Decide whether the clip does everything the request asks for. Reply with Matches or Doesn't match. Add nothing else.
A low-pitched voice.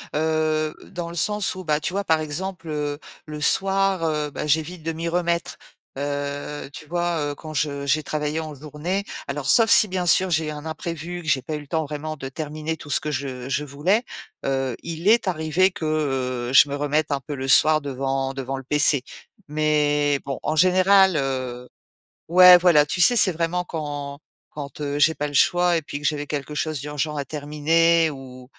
Doesn't match